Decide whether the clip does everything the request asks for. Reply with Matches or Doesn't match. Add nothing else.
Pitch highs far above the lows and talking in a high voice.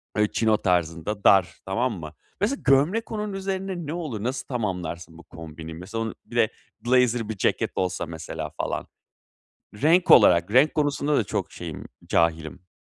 Doesn't match